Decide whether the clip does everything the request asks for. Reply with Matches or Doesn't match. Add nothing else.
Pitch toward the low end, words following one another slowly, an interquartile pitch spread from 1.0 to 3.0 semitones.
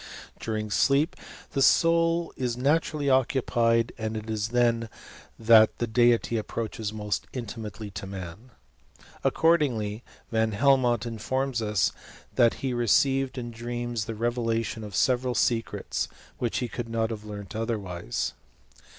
Matches